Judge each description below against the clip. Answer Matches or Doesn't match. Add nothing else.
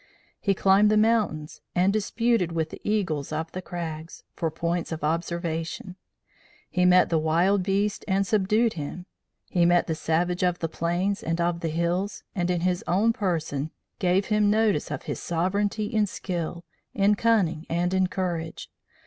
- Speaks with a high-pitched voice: Doesn't match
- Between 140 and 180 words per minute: Matches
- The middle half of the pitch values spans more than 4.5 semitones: Doesn't match